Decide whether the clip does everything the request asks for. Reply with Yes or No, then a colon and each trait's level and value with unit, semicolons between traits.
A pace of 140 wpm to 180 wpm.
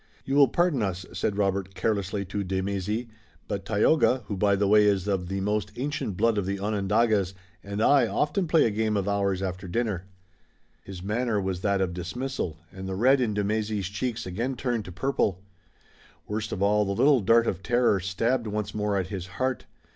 No: average, 200 wpm